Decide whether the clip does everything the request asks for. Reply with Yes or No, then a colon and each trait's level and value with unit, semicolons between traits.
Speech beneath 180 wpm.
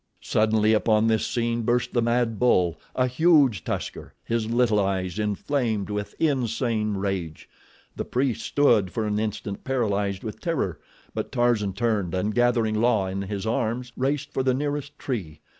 Yes: average, 155 wpm